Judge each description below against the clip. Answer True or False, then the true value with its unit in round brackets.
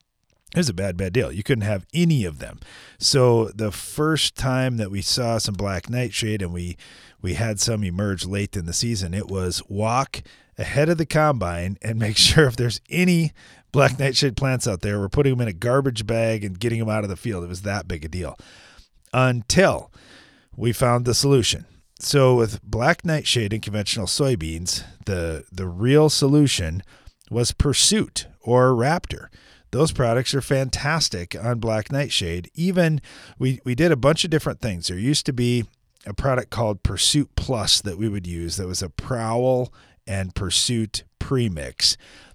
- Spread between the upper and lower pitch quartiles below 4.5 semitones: False (5.3 semitones)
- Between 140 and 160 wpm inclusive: False (180 wpm)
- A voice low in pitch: True (115 Hz)